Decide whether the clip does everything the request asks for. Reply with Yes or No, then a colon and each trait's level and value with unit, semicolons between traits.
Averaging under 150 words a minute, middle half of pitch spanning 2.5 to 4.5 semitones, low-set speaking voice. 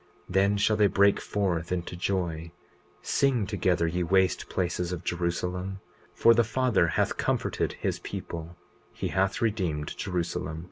Yes: average, 140 wpm; average, 2.8 semitones; very low, 90 Hz